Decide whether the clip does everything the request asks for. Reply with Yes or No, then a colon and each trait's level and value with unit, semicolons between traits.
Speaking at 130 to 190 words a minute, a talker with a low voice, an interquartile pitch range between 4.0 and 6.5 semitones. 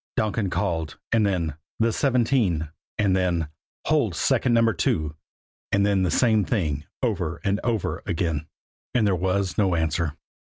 Yes: average, 165 wpm; very low, 95 Hz; average, 5.1 semitones